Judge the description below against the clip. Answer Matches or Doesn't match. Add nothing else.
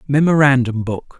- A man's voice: Matches